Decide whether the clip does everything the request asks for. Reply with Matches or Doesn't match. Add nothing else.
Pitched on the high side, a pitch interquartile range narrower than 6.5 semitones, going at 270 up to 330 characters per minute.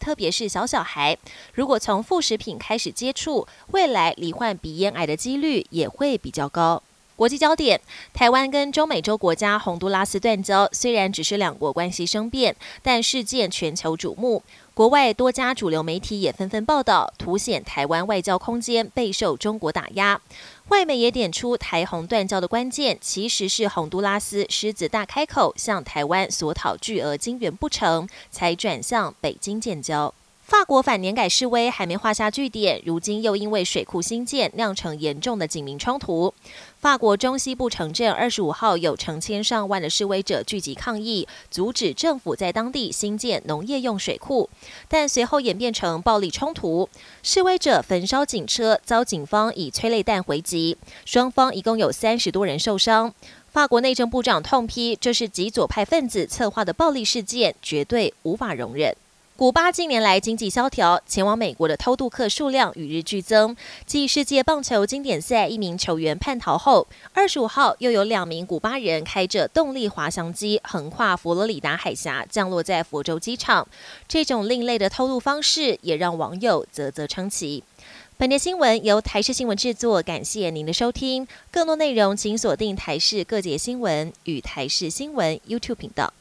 Matches